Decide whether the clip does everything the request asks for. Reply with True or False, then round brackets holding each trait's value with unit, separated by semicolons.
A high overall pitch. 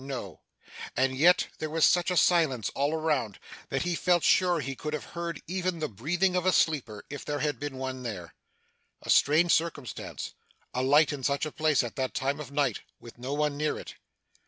False (150 Hz)